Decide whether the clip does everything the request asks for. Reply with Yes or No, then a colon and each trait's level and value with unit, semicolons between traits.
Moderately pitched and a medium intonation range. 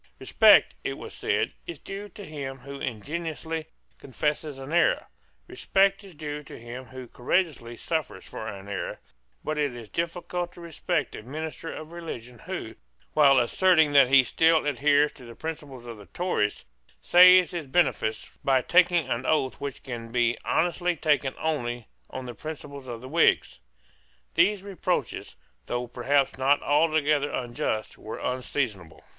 Yes: medium, 145 Hz; average, 4.8 semitones